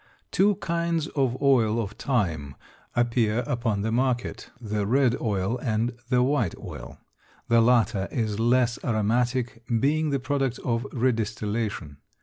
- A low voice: Yes, low, 120 Hz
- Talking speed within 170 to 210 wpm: No, slow, 135 wpm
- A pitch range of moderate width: Yes, average, 3.1 semitones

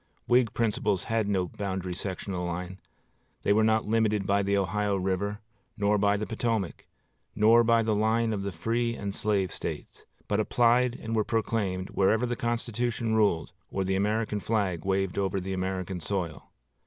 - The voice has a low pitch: Yes, low, 105 Hz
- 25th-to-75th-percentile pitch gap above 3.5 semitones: No, average, 2.9 semitones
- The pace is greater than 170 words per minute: No, average, 165 wpm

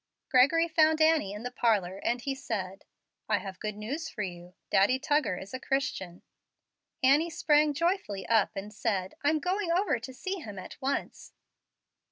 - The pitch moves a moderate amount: No, wide, 7.6 semitones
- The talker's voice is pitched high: Yes, very high, 255 Hz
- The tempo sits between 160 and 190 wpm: Yes, average, 170 wpm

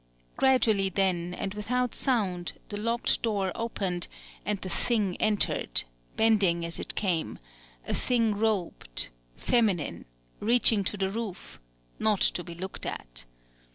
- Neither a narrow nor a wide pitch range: Yes, average, 3.8 semitones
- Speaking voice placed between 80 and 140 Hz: No, high, 200 Hz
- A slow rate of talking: Yes, slow, 130 wpm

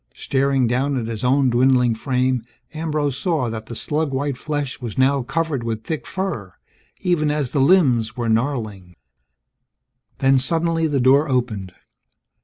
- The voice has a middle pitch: No, low, 130 Hz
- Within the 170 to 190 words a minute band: No, average, 150 wpm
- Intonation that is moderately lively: Yes, average, 3.8 semitones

